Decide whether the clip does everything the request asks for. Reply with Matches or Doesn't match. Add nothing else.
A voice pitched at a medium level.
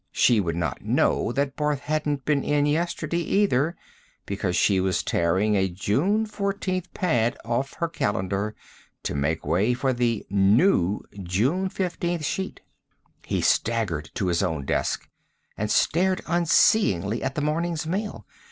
Doesn't match